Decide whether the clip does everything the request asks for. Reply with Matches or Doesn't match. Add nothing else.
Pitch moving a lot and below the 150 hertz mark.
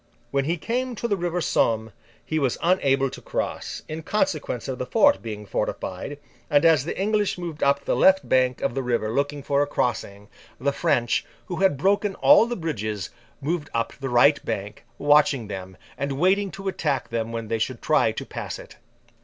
Matches